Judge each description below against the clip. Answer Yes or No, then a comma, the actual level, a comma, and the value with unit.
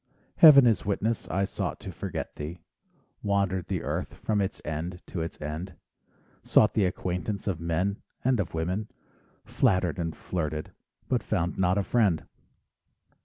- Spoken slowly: No, average, 150 wpm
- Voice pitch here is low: Yes, very low, 95 Hz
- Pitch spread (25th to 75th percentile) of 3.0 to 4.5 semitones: Yes, average, 3.5 semitones